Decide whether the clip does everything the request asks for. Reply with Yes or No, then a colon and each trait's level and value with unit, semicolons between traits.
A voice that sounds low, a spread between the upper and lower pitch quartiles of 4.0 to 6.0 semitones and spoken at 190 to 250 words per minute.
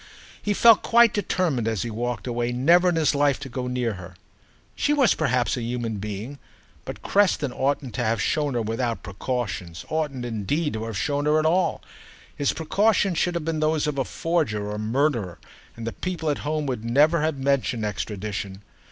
Yes: low, 130 Hz; wide, 5.6 semitones; average, 195 wpm